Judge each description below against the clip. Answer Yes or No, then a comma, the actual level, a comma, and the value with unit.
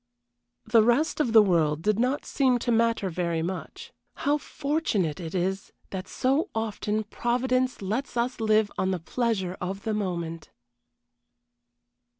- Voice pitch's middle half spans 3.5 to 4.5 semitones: No, average, 4.9 semitones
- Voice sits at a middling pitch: No, high, 215 Hz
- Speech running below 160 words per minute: Yes, average, 145 wpm